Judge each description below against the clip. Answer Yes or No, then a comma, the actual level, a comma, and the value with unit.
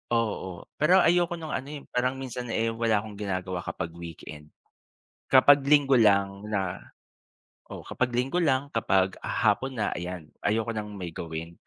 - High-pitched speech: No, low, 110 Hz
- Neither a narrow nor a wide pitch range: No, wide, 6.0 semitones